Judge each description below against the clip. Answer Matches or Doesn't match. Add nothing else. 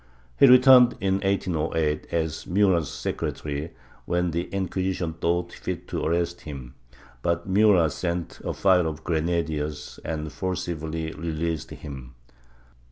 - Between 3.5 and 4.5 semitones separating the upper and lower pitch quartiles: Doesn't match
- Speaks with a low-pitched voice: Matches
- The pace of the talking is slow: Matches